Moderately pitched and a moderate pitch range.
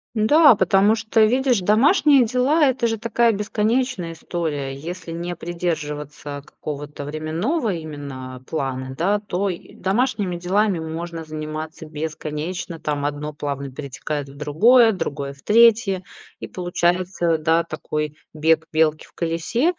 No: medium, 170 Hz; wide, 5.9 semitones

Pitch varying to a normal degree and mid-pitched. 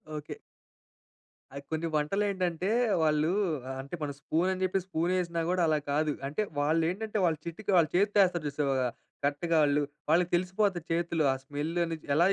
Yes: average, 3.3 semitones; medium, 165 Hz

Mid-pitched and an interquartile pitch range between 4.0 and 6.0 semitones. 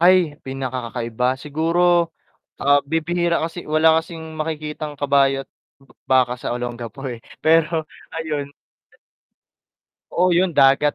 No: medium, 150 Hz; average, 3.4 semitones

